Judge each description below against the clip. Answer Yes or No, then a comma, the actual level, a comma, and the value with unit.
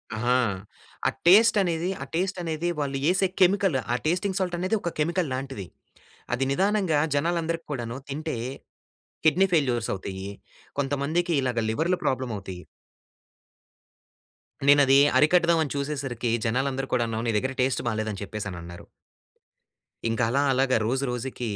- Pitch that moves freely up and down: Yes, wide, 5.9 semitones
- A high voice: No, medium, 140 Hz